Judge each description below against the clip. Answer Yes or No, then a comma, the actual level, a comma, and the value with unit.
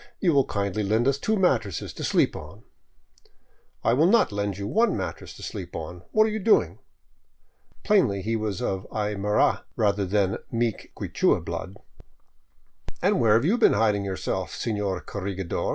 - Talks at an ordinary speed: Yes, average, 170 wpm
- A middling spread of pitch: Yes, average, 4.8 semitones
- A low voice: Yes, low, 105 Hz